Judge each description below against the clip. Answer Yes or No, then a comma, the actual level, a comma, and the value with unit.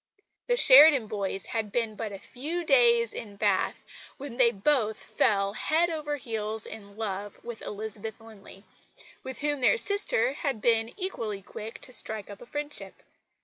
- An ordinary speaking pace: Yes, average, 160 wpm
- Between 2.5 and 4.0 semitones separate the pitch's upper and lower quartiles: No, average, 5.0 semitones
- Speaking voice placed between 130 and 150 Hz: No, high, 225 Hz